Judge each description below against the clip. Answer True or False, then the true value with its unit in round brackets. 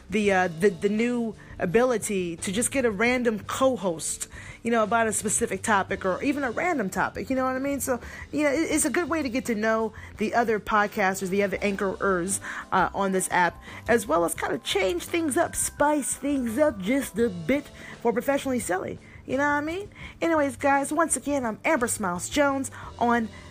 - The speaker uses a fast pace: True (210 wpm)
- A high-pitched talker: True (235 Hz)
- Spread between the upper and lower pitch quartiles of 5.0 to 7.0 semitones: True (5.6 semitones)